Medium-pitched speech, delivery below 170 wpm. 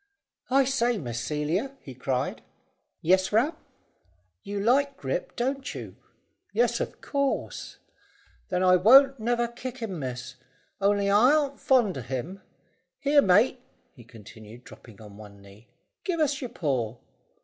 No: high, 200 Hz; average, 140 wpm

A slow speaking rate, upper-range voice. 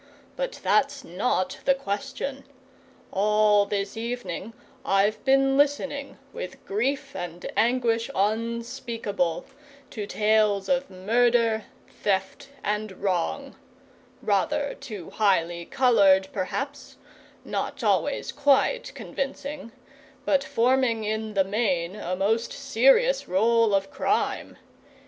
Yes: slow, 105 wpm; high, 220 Hz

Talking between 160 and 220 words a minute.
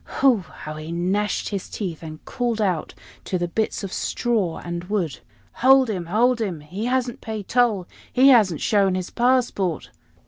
Yes: average, 170 wpm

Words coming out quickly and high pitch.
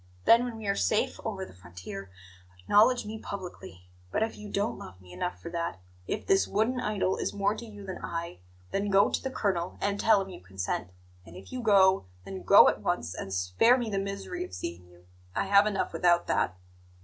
Yes: fast, 215 wpm; high, 195 Hz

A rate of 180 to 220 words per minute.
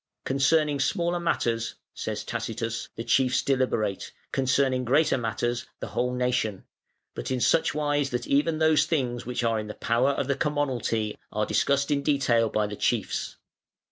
No: average, 160 wpm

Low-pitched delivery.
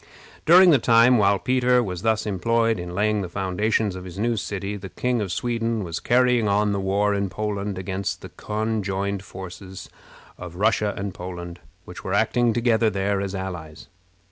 Yes: low, 100 Hz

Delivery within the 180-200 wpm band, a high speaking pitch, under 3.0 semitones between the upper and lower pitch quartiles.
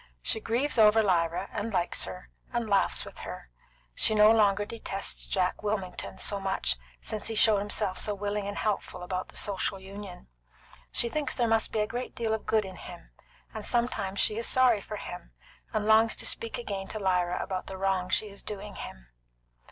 Yes: average, 195 wpm; high, 205 Hz; narrow, 2.5 semitones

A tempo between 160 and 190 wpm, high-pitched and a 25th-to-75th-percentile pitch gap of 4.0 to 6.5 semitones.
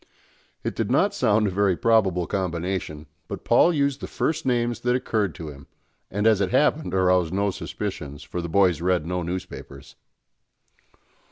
No: average, 165 wpm; very low, 95 Hz; average, 4.4 semitones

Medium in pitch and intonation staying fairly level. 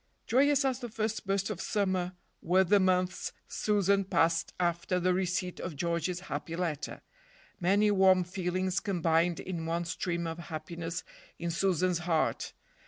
Yes: medium, 180 Hz; narrow, 2.3 semitones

